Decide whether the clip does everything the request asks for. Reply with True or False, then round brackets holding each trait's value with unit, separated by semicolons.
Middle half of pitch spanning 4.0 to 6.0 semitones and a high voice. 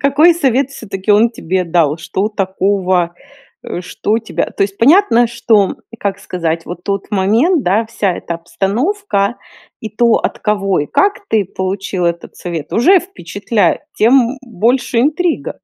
True (4.7 semitones; 210 Hz)